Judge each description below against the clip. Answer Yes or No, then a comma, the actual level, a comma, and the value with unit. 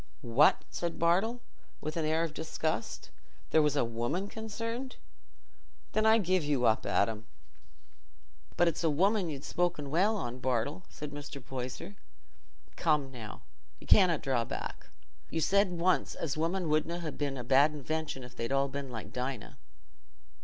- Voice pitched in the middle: Yes, medium, 155 Hz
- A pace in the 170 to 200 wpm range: No, average, 160 wpm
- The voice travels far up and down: No, average, 4.8 semitones